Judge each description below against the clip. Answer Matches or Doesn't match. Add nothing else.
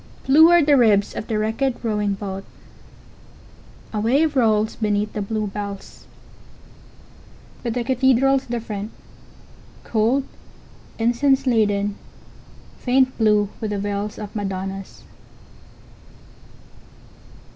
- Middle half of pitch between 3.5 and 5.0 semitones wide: Matches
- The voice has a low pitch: Doesn't match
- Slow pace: Matches